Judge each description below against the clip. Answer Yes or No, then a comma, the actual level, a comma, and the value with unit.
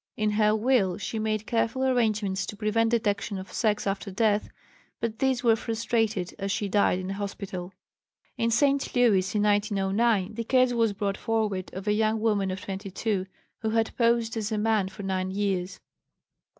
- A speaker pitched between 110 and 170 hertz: No, high, 210 Hz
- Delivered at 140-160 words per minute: No, average, 175 wpm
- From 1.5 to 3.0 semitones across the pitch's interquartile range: Yes, narrow, 2.5 semitones